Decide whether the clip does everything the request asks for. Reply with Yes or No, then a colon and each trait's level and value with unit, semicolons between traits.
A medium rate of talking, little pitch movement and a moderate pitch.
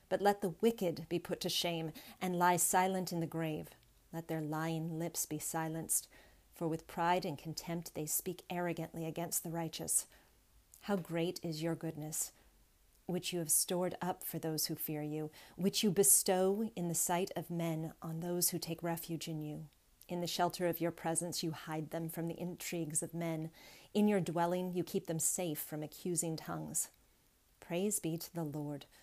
Yes: average, 185 wpm; narrow, 1.7 semitones; medium, 170 Hz